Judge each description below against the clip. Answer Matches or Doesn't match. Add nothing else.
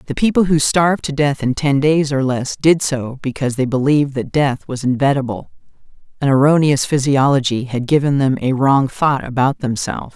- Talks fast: Doesn't match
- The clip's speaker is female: Matches